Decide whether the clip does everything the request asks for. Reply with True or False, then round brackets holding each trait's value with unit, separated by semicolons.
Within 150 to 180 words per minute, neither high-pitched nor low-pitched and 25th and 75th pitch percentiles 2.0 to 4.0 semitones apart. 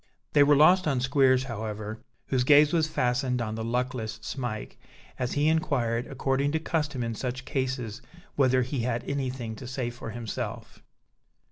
False (160 wpm; 130 Hz; 3.0 semitones)